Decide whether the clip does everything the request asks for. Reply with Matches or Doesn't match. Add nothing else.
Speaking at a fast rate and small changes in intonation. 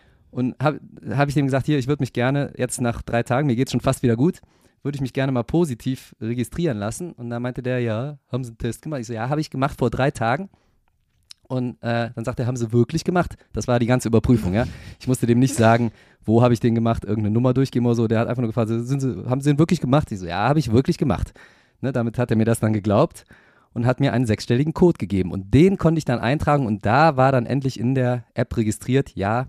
Doesn't match